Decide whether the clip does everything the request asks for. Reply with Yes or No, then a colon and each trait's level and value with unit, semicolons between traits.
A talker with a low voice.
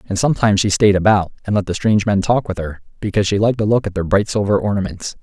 Yes: low, 100 Hz